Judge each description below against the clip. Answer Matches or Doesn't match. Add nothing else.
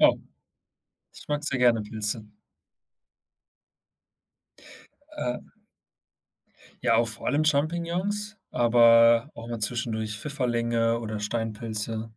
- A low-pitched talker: Matches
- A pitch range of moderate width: Matches